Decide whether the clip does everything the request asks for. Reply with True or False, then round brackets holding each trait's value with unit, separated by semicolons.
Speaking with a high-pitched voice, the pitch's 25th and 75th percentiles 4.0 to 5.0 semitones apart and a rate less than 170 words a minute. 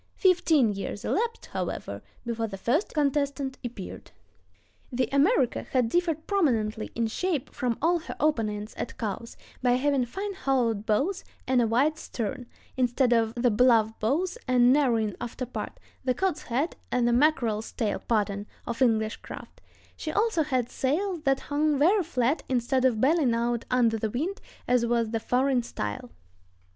True (250 Hz; 4.6 semitones; 150 wpm)